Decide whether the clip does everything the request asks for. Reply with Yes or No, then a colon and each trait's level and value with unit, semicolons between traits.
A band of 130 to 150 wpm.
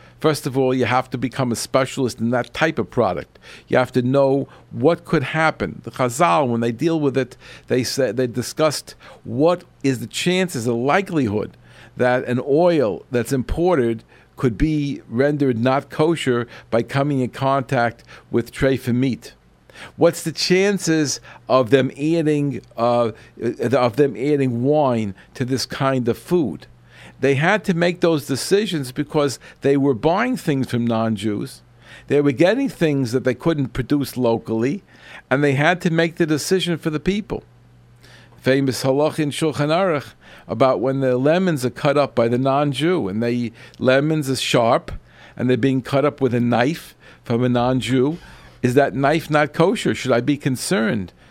No: average, 170 wpm